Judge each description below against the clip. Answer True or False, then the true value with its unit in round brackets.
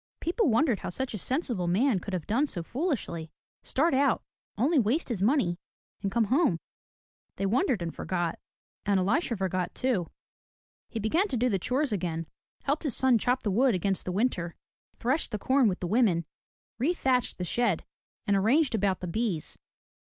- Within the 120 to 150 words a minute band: False (175 wpm)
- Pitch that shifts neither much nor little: False (6.0 semitones)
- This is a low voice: False (225 Hz)